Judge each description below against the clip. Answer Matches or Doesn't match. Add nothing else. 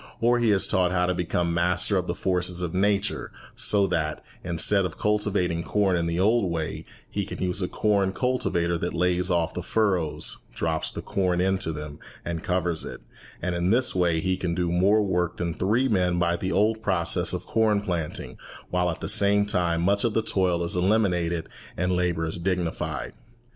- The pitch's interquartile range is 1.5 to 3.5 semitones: Matches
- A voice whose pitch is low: Matches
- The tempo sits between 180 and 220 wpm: Matches